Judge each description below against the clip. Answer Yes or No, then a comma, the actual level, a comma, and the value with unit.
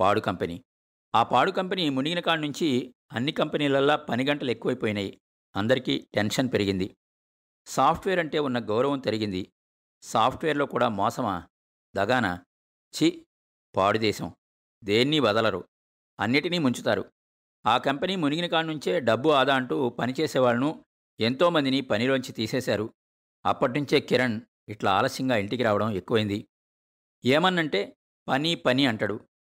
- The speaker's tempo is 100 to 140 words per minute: Yes, average, 115 wpm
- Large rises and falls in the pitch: Yes, wide, 6.7 semitones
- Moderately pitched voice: No, low, 125 Hz